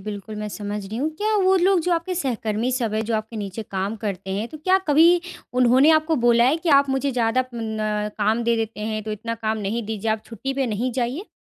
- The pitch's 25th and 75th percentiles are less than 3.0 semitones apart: No, average, 4.5 semitones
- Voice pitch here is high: Yes, high, 230 Hz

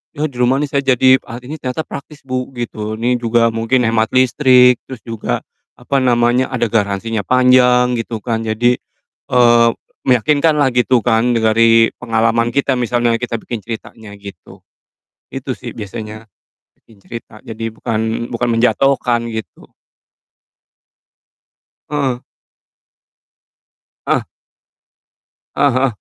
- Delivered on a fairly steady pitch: Yes, narrow, 2.0 semitones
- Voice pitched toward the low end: Yes, low, 120 Hz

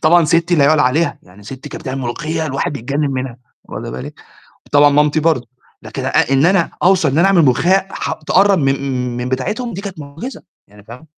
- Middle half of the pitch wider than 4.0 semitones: Yes, average, 4.4 semitones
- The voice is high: No, medium, 150 Hz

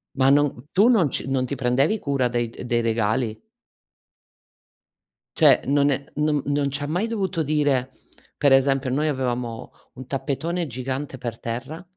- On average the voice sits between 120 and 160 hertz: Yes, low, 135 Hz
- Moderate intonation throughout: Yes, average, 3.0 semitones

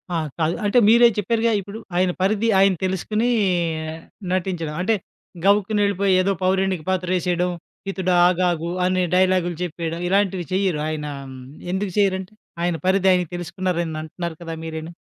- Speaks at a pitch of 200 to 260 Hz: No, medium, 185 Hz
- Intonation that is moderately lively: No, narrow, 2.2 semitones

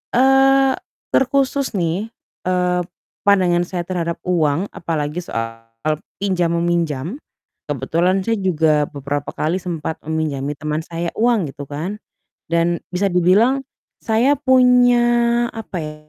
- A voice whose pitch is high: No, medium, 180 Hz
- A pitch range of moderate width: No, wide, 6.2 semitones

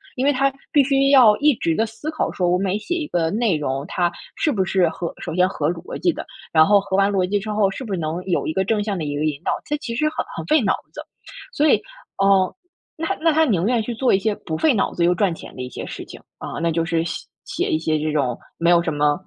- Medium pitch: No, high, 195 Hz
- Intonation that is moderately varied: No, wide, 6.5 semitones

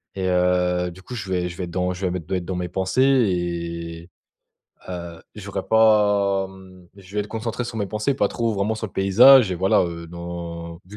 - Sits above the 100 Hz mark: No, very low, 95 Hz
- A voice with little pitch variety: No, average, 3.1 semitones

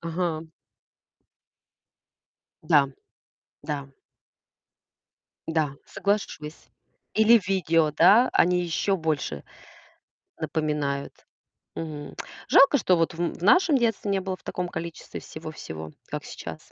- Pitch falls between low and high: Yes, medium, 165 Hz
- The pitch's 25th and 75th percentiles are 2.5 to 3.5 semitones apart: No, average, 4.2 semitones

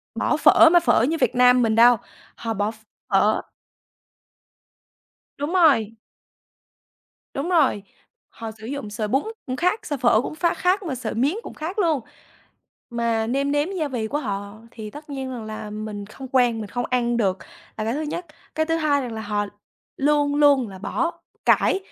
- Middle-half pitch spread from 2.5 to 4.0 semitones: No, average, 5.2 semitones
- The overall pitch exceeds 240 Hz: Yes, very high, 250 Hz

